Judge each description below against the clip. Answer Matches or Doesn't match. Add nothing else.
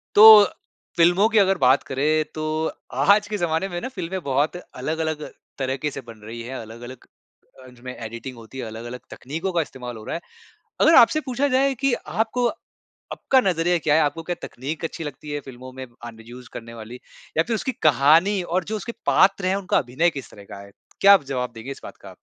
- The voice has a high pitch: Doesn't match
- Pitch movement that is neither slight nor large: Doesn't match